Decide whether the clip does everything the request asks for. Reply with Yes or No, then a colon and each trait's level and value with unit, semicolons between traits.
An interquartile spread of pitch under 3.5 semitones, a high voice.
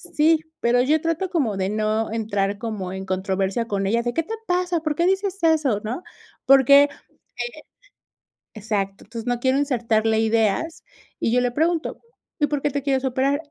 No: wide, 6.2 semitones; high, 245 Hz